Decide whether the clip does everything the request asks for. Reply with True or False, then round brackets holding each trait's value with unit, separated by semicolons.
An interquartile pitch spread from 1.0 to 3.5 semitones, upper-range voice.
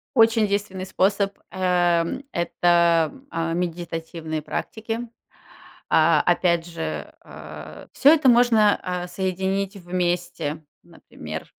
False (3.2 semitones; 180 Hz)